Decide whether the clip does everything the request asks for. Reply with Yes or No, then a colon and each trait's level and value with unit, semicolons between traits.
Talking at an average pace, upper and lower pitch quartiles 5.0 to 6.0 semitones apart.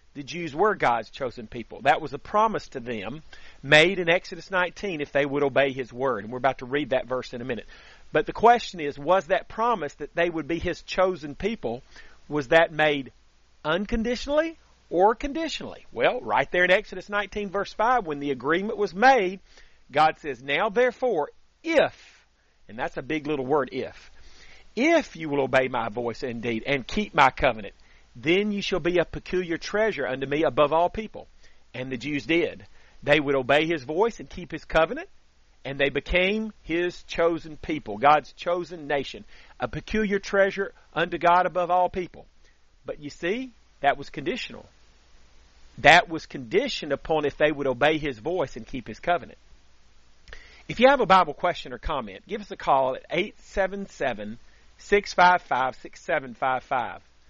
Yes: average, 170 wpm; wide, 5.6 semitones